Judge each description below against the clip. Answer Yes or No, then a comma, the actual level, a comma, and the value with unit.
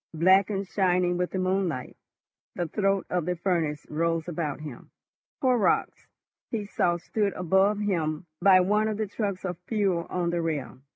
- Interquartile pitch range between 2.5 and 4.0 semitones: Yes, average, 2.9 semitones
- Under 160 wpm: No, average, 165 wpm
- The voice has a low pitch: No, medium, 180 Hz